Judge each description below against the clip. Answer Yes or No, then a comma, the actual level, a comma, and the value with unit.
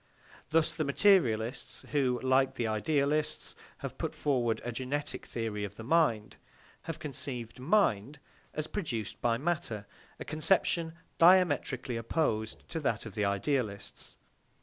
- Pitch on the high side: No, low, 130 Hz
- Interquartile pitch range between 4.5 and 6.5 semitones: Yes, wide, 5.4 semitones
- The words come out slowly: Yes, slow, 130 wpm